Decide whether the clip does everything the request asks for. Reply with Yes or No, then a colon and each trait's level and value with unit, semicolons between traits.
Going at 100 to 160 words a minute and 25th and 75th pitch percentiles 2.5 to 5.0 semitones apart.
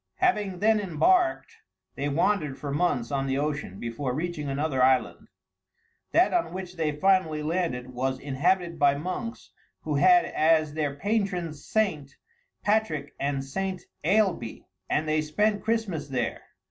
No: average, 140 wpm; wide, 5.6 semitones